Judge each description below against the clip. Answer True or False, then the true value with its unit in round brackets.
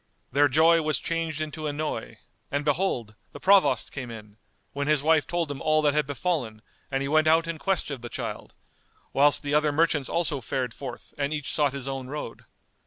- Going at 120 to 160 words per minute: False (200 wpm)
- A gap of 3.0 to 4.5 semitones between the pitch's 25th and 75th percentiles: False (2.5 semitones)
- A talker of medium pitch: True (145 Hz)